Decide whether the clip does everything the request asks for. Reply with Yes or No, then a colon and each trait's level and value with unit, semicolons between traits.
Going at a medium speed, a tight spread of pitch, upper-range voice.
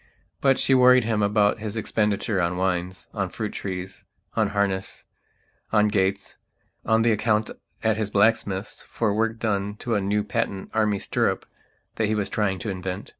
No: average, 170 wpm; narrow, 2.3 semitones; low, 105 Hz